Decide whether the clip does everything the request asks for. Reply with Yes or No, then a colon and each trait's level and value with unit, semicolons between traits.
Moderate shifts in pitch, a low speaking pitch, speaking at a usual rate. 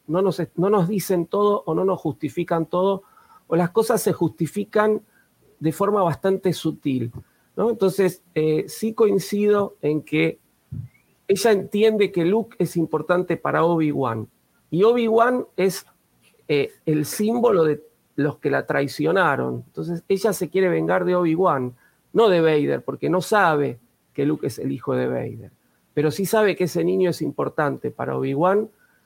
No: average, 4.7 semitones; medium, 180 Hz; average, 155 wpm